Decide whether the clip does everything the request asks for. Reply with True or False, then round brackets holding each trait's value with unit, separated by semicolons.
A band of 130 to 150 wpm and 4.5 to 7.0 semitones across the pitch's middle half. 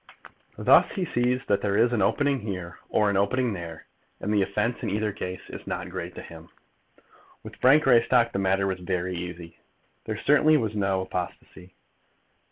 False (175 wpm; 4.8 semitones)